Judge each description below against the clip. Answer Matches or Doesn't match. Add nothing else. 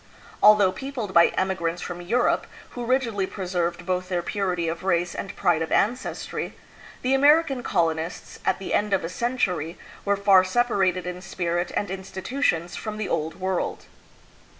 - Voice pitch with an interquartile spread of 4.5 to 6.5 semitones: Doesn't match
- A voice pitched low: Doesn't match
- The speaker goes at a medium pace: Matches